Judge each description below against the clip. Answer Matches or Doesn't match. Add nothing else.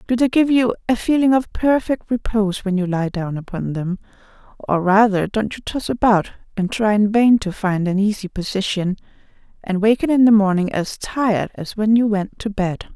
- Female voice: Matches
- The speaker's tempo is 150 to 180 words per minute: Doesn't match